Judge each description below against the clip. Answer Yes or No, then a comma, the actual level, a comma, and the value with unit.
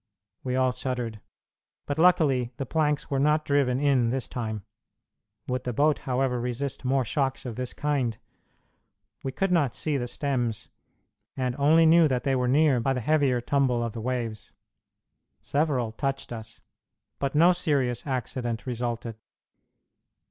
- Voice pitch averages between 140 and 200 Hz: No, low, 130 Hz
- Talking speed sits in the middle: Yes, average, 150 wpm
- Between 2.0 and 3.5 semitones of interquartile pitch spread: Yes, average, 2.8 semitones